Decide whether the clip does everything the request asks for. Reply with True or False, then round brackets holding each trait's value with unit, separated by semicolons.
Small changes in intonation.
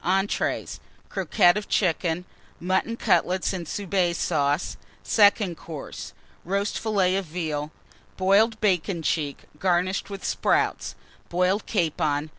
False (3.2 semitones)